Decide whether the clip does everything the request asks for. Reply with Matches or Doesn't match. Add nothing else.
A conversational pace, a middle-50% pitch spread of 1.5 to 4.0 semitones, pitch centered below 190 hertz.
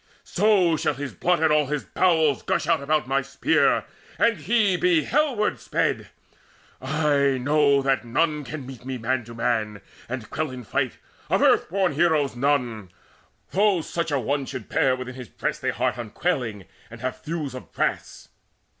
Doesn't match